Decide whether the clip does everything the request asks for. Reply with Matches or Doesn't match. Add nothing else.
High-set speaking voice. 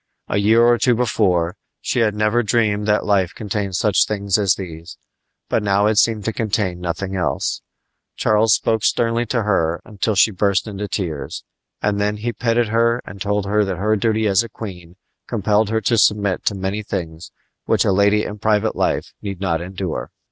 Doesn't match